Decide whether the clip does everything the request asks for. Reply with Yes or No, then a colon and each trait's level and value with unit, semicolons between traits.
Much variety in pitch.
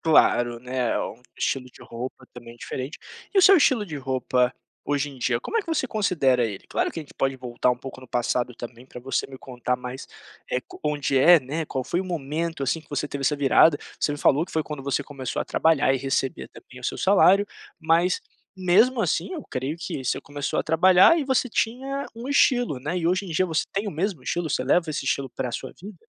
Yes: wide, 6.0 semitones